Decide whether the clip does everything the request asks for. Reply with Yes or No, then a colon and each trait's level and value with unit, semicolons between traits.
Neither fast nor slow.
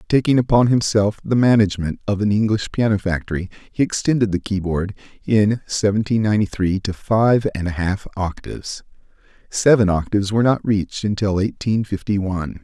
Yes: average, 155 wpm